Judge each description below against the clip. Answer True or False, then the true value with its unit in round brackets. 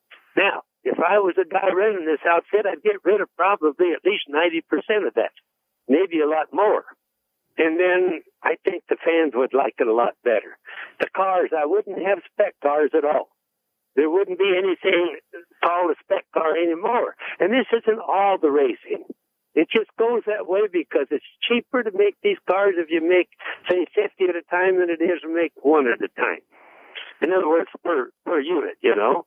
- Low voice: False (200 Hz)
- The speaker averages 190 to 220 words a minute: True (200 wpm)